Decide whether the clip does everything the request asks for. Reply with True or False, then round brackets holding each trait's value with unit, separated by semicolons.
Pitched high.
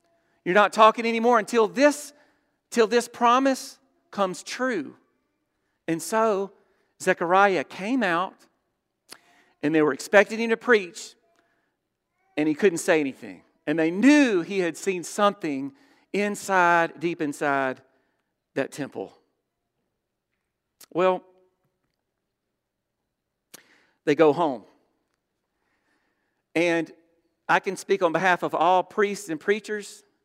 True (200 Hz)